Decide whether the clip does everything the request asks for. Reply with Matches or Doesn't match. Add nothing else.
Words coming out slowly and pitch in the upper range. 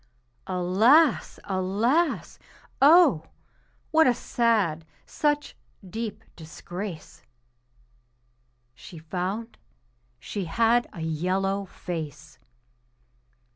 Matches